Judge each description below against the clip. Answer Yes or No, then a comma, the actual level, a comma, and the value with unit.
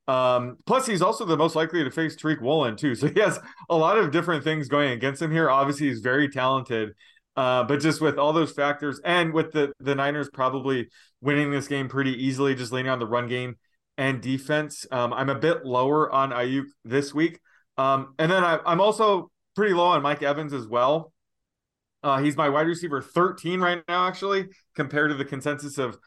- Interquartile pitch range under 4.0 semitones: Yes, average, 3.4 semitones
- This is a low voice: No, medium, 145 Hz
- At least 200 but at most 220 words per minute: Yes, fast, 205 wpm